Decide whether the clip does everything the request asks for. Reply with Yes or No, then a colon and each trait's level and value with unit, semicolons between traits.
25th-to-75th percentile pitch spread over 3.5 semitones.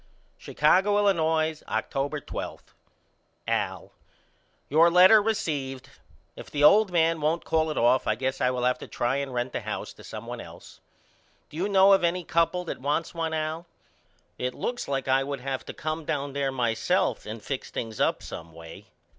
Yes: average, 4.3 semitones